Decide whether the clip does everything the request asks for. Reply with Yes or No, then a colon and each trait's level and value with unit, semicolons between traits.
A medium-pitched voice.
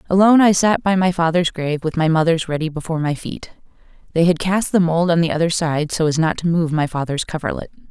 Yes: medium, 165 Hz